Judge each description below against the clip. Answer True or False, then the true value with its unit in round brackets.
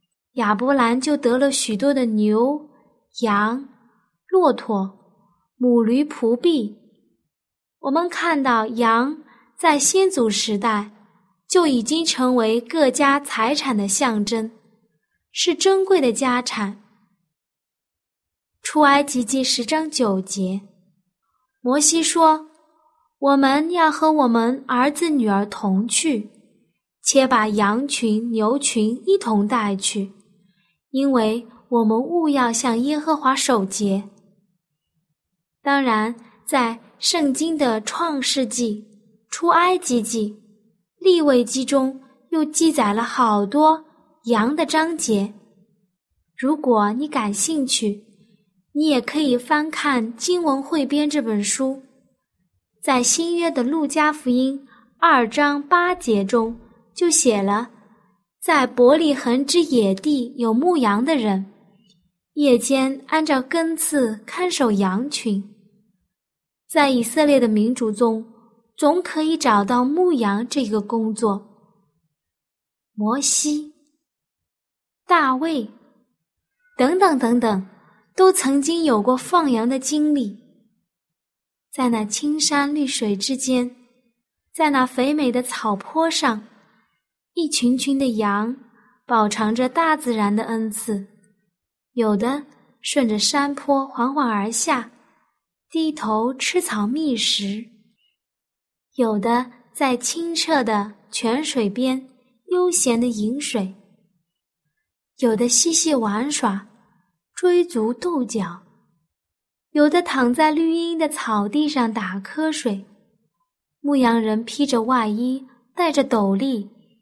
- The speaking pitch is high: True (245 Hz)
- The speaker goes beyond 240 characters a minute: False (155 characters per minute)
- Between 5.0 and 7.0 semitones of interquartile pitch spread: True (5.3 semitones)